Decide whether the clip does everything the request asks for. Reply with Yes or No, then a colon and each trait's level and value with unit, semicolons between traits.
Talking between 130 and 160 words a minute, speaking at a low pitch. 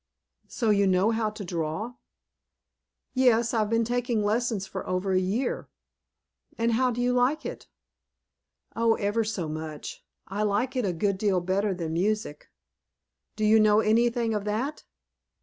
No: average, 155 wpm; high, 215 Hz